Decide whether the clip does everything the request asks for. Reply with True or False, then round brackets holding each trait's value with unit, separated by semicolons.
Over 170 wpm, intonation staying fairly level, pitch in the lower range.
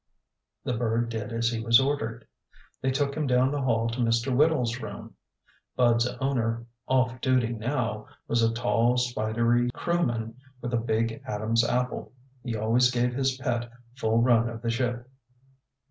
False (160 wpm; 1.8 semitones; 120 Hz)